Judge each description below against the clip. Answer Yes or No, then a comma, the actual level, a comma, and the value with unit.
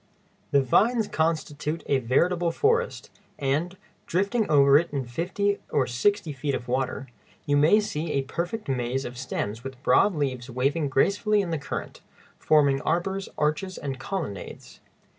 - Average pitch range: No, wide, 5.7 semitones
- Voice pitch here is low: No, medium, 150 Hz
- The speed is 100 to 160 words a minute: Yes, average, 150 wpm